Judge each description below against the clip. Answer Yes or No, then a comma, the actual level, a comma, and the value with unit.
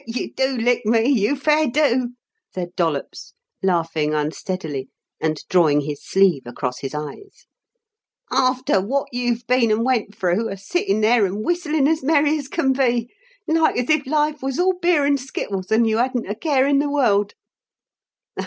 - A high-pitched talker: Yes, high, 240 Hz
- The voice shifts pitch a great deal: Yes, wide, 6.7 semitones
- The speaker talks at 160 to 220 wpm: Yes, average, 170 wpm